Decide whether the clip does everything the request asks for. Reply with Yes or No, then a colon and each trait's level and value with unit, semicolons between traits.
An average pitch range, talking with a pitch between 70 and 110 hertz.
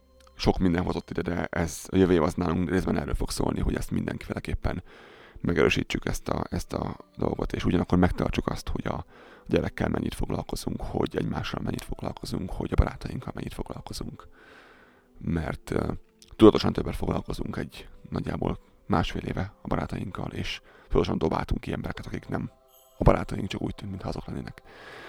No: wide, 7.1 semitones; very low, 95 Hz